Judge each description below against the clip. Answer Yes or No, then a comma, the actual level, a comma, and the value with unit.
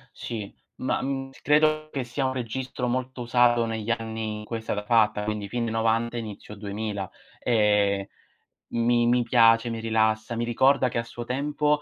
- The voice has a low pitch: Yes, low, 115 Hz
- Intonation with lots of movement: No, narrow, 2.4 semitones